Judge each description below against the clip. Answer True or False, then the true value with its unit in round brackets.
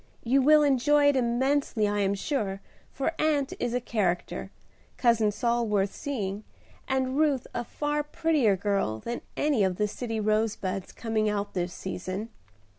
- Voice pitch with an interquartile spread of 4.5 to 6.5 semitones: True (5.2 semitones)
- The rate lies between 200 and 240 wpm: False (160 wpm)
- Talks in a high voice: True (230 Hz)